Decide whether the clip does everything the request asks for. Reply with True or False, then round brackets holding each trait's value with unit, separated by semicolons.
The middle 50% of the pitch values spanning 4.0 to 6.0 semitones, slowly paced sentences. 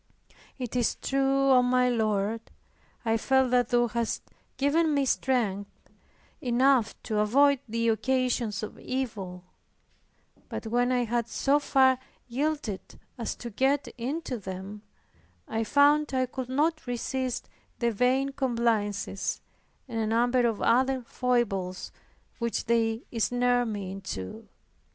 False (3.0 semitones; 125 wpm)